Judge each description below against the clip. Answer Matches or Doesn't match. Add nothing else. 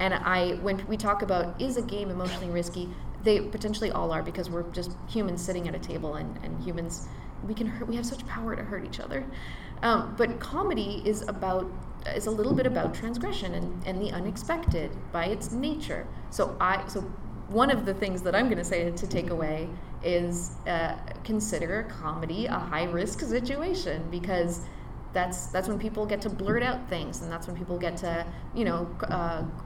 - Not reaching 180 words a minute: Doesn't match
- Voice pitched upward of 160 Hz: Matches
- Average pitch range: Matches